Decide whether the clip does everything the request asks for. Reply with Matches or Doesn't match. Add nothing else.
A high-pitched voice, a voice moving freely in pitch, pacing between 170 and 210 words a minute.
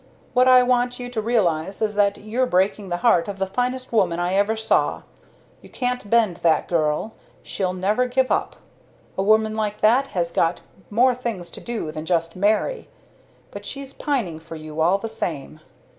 Matches